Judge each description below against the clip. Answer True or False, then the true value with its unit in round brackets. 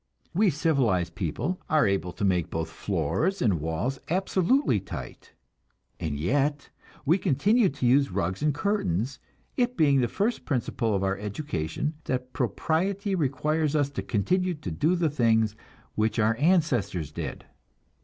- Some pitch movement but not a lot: False (8.9 semitones)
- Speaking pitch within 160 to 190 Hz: False (135 Hz)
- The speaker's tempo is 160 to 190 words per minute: False (145 wpm)